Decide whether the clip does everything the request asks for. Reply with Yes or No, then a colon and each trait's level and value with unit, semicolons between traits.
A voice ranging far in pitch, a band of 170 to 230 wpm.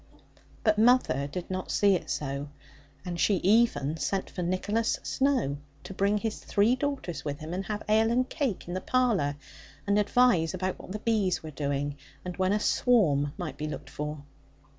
Yes: wide, 6.2 semitones; average, 185 wpm